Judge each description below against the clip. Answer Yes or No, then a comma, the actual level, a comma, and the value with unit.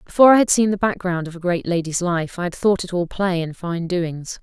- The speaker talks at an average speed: No, fast, 270 wpm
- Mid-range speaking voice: Yes, medium, 180 Hz